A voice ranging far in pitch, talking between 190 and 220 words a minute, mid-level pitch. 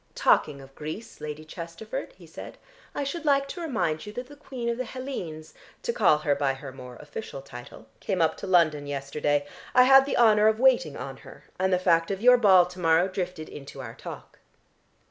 Yes: wide, 8.4 semitones; fast, 205 wpm; medium, 180 Hz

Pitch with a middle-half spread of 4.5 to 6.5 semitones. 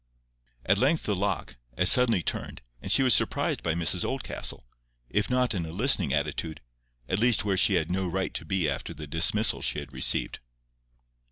Yes: average, 5.3 semitones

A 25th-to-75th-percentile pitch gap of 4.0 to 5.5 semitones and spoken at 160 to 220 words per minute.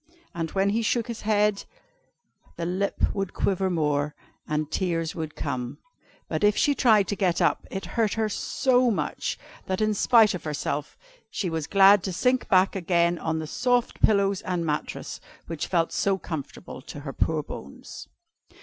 Yes: average, 4.6 semitones; average, 170 wpm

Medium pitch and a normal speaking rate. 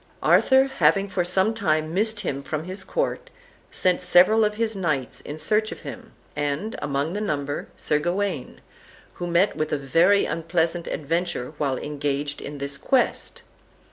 Yes: medium, 170 Hz; average, 160 wpm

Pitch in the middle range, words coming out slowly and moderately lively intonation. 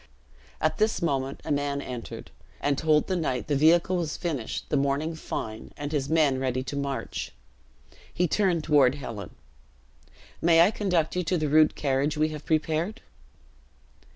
No: medium, 150 Hz; average, 160 wpm; average, 3.1 semitones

